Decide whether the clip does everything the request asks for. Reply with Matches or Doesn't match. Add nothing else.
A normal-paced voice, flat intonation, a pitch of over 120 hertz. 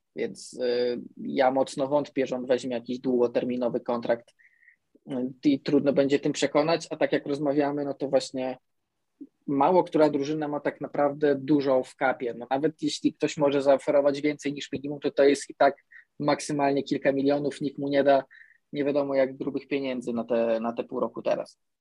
Doesn't match